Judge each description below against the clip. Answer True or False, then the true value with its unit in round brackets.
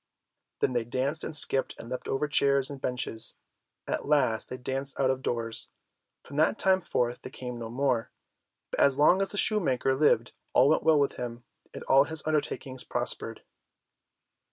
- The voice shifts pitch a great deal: False (3.1 semitones)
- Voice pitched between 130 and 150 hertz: True (135 Hz)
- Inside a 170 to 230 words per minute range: True (180 wpm)